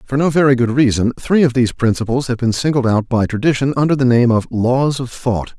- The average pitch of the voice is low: Yes, low, 125 Hz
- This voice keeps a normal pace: No, fast, 235 wpm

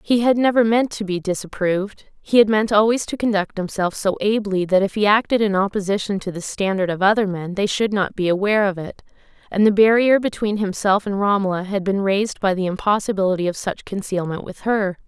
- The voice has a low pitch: No, high, 200 Hz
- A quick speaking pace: Yes, fast, 210 wpm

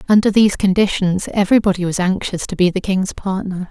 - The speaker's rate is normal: Yes, average, 180 wpm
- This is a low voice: No, high, 190 Hz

